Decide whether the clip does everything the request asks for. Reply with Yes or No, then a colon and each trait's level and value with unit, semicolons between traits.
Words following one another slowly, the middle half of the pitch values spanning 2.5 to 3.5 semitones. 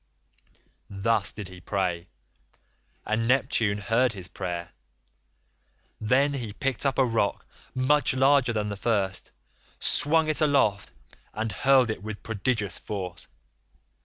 No: slow, 130 wpm; average, 4.7 semitones